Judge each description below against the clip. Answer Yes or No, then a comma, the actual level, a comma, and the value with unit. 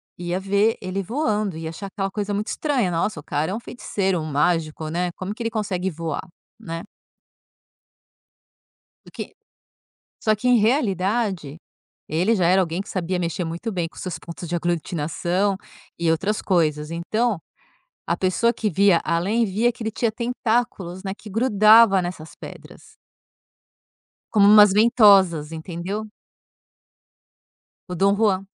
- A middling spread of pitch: Yes, average, 4.1 semitones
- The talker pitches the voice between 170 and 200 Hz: Yes, high, 190 Hz